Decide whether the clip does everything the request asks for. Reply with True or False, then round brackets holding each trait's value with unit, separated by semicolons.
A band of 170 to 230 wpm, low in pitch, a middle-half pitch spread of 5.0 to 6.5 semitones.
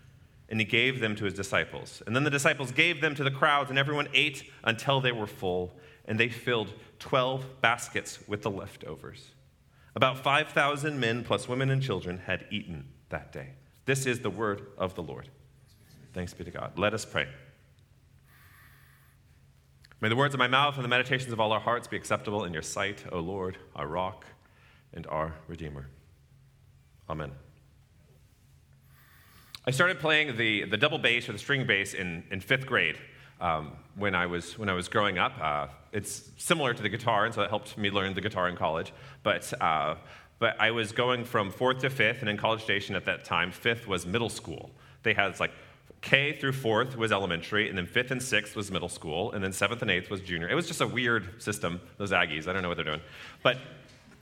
True (200 wpm; 105 Hz; 5.6 semitones)